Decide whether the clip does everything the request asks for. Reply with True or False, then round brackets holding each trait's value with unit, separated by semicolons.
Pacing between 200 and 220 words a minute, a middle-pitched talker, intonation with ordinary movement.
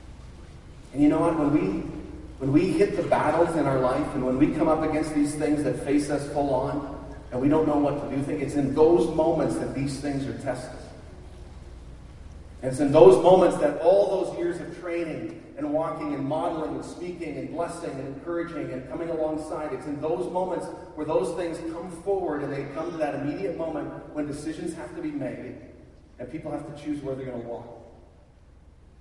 True (205 wpm; 150 Hz; 3.7 semitones)